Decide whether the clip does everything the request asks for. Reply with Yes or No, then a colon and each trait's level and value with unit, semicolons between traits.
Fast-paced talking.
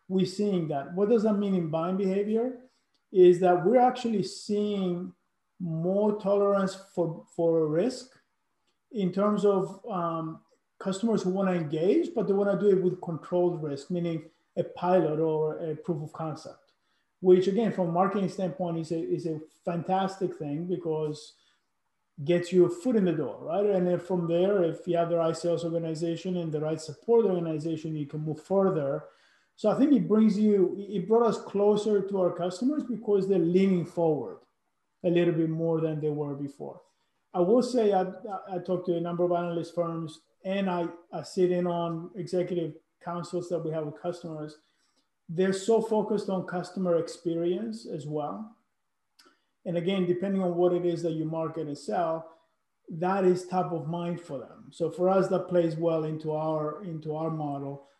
No: average, 180 wpm